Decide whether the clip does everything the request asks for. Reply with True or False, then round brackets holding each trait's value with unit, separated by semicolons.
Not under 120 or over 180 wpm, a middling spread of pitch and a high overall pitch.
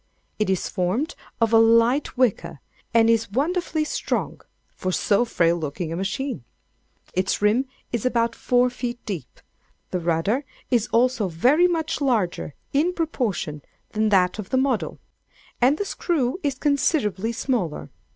False (145 wpm; 5.8 semitones; 230 Hz)